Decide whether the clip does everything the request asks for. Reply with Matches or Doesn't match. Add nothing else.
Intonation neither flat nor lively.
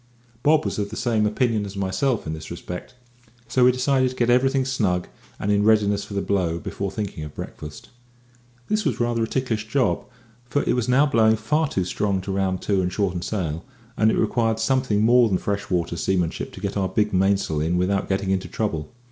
Matches